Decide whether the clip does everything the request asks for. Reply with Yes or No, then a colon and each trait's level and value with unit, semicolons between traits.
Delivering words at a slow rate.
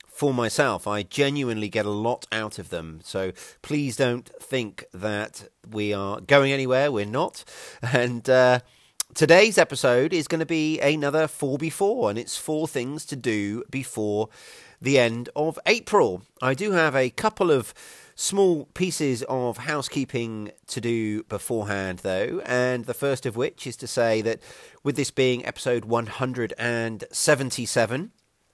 No: average, 155 wpm